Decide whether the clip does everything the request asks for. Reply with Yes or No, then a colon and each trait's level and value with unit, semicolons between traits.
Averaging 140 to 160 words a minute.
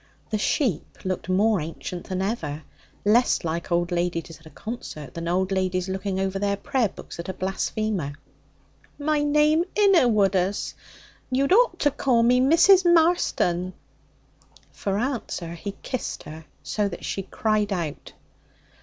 Yes: average, 145 wpm